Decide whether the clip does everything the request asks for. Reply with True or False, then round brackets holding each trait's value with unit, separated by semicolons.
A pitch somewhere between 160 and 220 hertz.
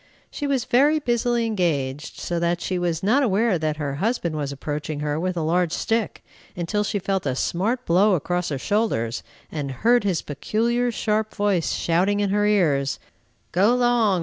True (185 Hz)